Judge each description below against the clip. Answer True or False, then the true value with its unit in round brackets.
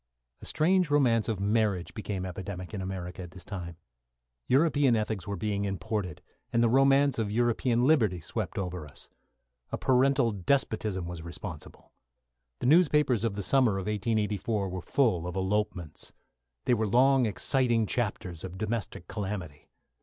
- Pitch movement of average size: True (4.7 semitones)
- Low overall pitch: True (105 Hz)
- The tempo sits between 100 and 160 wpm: True (150 wpm)